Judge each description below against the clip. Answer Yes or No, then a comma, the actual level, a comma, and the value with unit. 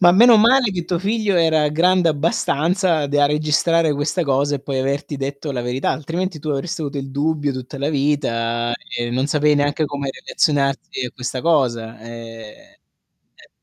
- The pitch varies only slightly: No, average, 3.5 semitones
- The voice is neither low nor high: Yes, medium, 145 Hz